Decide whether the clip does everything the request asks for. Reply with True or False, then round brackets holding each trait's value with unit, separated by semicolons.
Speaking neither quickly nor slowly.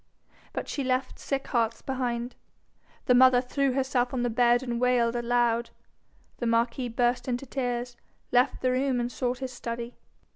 True (160 wpm)